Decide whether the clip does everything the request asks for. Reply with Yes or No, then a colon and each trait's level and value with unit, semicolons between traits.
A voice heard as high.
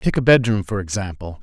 No: low, 100 Hz